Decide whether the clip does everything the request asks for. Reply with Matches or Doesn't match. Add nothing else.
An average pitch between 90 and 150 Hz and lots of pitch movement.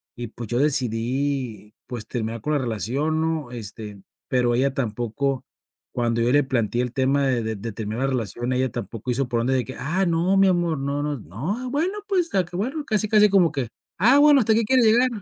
Matches